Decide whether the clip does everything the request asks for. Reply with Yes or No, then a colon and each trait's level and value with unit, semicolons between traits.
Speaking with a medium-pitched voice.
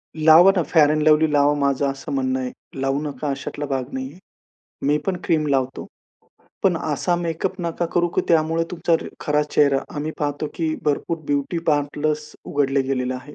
Yes: medium, 150 Hz